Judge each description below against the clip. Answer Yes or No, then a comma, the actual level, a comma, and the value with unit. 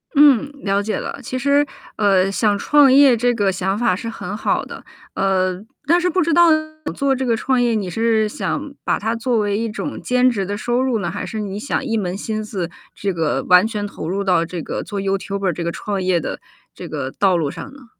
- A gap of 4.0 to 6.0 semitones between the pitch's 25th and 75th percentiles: Yes, average, 4.4 semitones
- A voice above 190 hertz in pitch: Yes, high, 210 Hz